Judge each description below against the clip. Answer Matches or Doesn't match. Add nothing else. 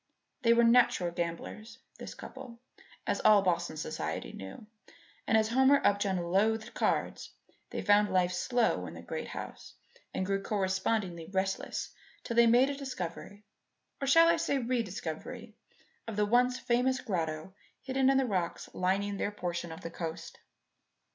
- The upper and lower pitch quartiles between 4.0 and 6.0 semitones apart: Matches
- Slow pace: Doesn't match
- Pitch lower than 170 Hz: Doesn't match